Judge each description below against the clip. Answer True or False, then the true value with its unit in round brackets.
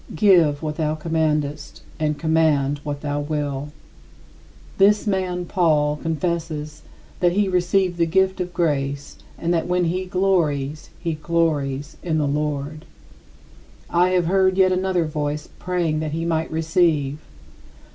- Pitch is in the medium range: True (160 Hz)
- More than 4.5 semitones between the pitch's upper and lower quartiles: False (3.2 semitones)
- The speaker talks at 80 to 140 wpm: True (135 wpm)